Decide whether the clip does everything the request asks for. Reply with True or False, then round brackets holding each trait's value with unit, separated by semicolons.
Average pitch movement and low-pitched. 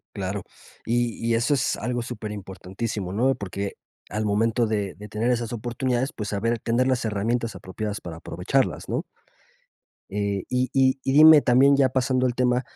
True (3.6 semitones; 115 Hz)